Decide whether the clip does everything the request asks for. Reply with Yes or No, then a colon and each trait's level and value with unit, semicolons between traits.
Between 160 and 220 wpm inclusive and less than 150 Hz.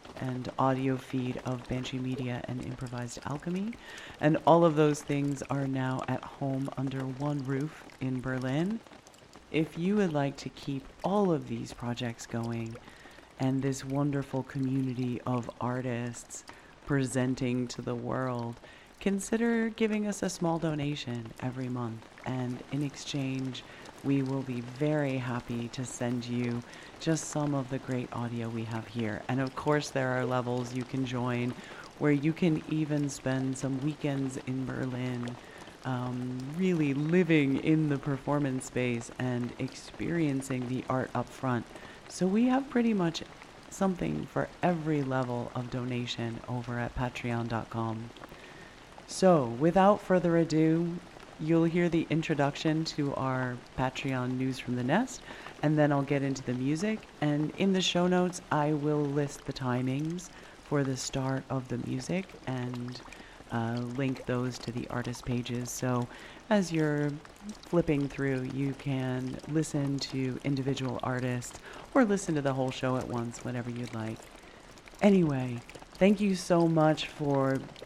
No: average, 145 wpm; low, 135 Hz